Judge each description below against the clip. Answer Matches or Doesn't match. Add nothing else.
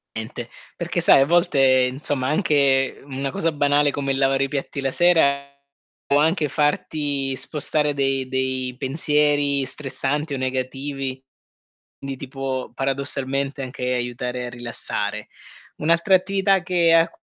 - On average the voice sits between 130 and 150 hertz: Matches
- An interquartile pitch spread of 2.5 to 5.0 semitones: Doesn't match